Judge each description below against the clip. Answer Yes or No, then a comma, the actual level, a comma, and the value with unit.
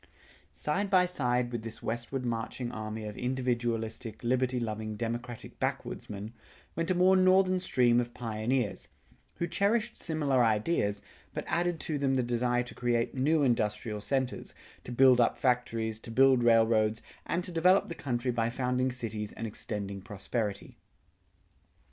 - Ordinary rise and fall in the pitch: Yes, average, 3.2 semitones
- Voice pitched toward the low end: Yes, low, 120 Hz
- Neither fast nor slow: Yes, average, 150 wpm